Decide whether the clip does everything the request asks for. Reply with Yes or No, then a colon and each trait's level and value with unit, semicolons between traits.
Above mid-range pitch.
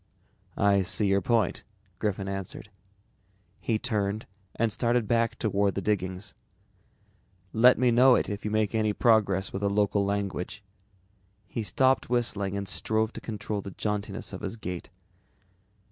No: low, 105 Hz